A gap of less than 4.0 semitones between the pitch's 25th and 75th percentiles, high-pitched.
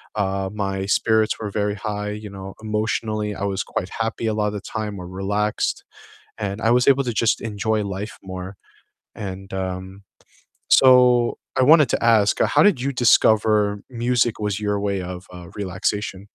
No: narrow, 2.5 semitones; low, 105 Hz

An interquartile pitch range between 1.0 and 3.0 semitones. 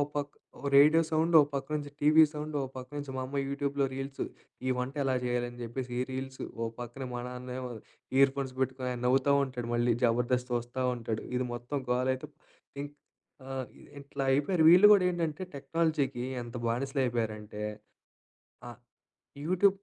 Yes: narrow, 2.6 semitones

